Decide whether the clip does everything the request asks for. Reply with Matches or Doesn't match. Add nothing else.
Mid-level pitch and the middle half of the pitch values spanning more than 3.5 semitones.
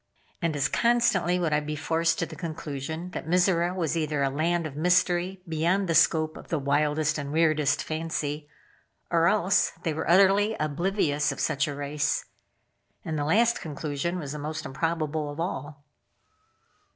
Doesn't match